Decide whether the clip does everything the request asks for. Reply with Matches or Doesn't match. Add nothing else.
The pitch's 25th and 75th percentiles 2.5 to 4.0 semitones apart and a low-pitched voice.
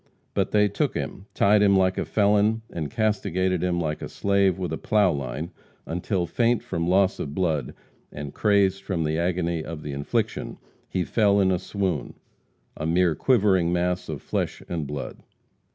Matches